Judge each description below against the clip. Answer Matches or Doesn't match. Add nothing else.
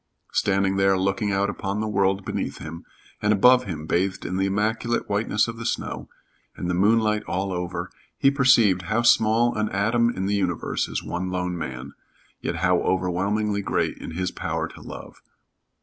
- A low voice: Matches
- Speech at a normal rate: Matches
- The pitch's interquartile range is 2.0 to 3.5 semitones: Matches